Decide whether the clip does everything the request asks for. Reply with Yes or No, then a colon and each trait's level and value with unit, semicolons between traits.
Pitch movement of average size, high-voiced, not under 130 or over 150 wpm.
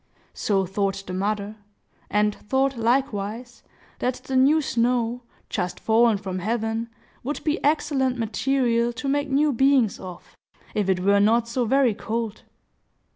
Yes: average, 4.2 semitones; high, 235 Hz; average, 140 wpm